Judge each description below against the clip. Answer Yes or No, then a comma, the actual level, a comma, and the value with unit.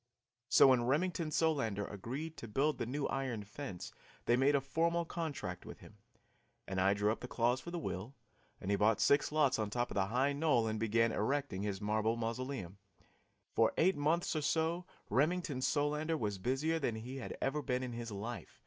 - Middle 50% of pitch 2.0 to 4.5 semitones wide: No, average, 5.3 semitones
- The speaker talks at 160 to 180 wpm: No, average, 195 wpm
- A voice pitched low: Yes, low, 130 Hz